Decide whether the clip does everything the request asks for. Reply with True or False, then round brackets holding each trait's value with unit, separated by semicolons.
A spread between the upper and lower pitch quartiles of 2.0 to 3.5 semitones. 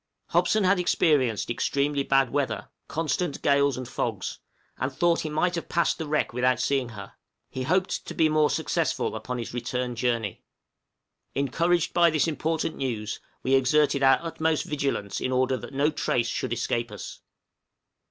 False (4.0 semitones)